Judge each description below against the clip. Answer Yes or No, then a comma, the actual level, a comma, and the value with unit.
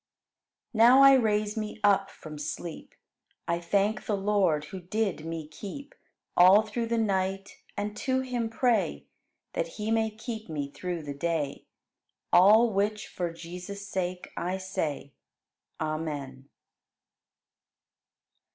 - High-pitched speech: Yes, high, 195 Hz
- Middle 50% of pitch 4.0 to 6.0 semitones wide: Yes, average, 4.6 semitones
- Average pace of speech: No, slow, 130 wpm